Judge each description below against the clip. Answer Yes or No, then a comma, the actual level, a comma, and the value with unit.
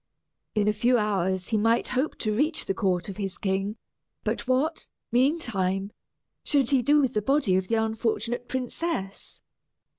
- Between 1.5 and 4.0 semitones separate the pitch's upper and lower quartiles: No, average, 4.8 semitones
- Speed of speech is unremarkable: Yes, average, 160 wpm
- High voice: Yes, high, 220 Hz